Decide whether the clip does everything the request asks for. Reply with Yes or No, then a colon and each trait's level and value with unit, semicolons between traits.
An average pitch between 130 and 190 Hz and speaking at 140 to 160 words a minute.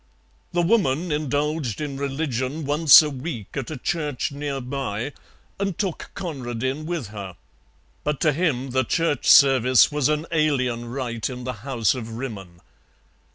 Yes: low, 135 Hz; average, 150 wpm